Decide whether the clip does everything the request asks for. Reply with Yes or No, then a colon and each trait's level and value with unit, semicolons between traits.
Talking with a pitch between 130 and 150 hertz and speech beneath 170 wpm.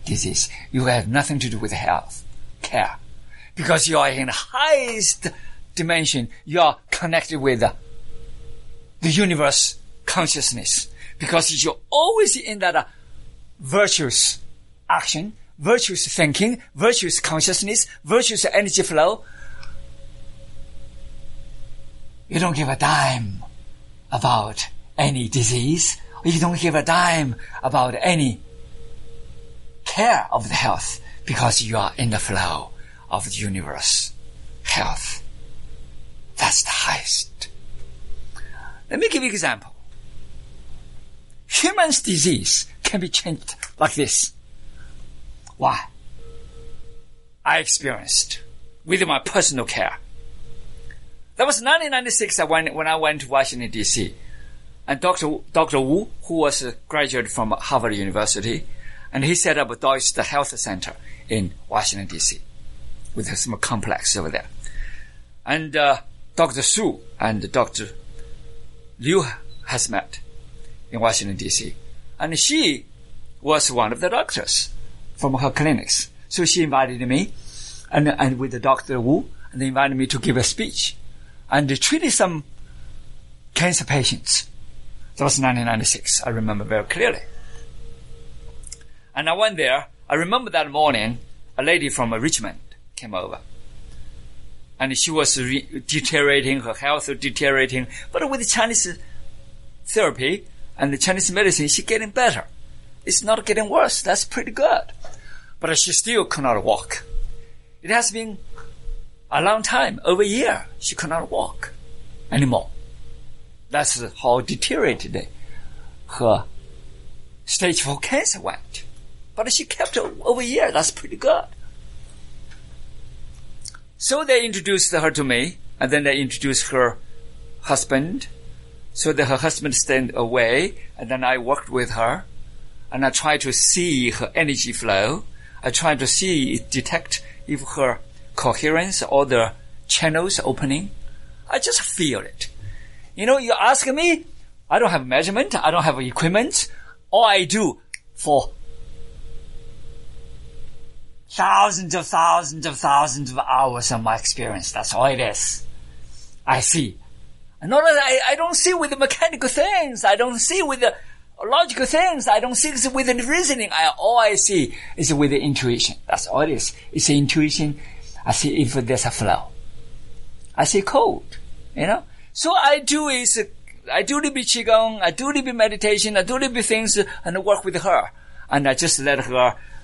Yes: medium, 140 Hz; average, 140 wpm